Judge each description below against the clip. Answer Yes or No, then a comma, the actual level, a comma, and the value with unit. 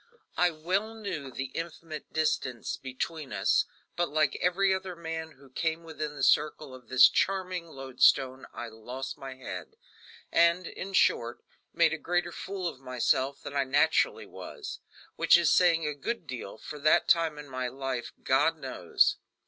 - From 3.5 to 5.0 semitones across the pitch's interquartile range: Yes, average, 4.4 semitones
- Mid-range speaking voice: Yes, medium, 155 Hz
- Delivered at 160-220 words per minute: Yes, average, 165 wpm